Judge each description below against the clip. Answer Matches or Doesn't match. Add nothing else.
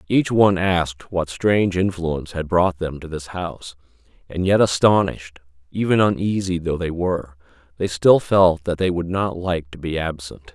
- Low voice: Matches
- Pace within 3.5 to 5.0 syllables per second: Matches